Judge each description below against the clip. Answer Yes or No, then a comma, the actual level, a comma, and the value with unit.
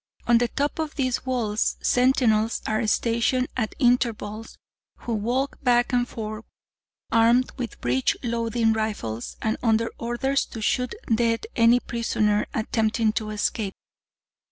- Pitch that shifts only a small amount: Yes, narrow, 2.1 semitones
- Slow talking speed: Yes, slow, 130 wpm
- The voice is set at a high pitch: Yes, high, 230 Hz